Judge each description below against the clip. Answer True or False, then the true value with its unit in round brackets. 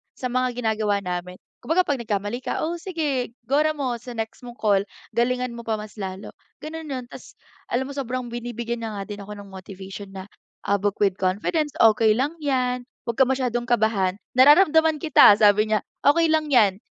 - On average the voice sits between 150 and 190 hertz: False (240 Hz)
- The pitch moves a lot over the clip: False (4.7 semitones)